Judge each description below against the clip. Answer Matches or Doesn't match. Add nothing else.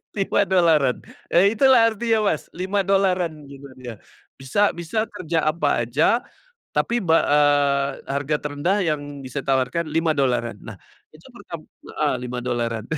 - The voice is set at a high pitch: Doesn't match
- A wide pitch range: Matches